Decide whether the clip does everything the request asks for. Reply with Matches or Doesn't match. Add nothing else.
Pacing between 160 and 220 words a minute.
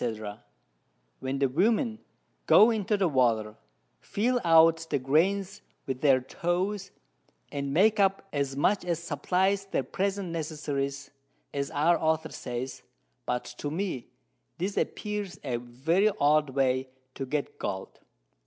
Doesn't match